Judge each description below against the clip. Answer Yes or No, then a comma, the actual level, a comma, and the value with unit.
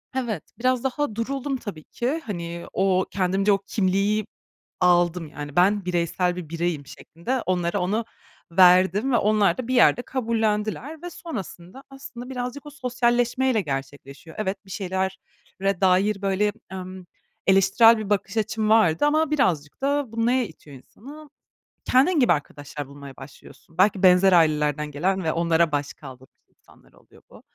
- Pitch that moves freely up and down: Yes, wide, 5.8 semitones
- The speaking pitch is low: No, high, 195 Hz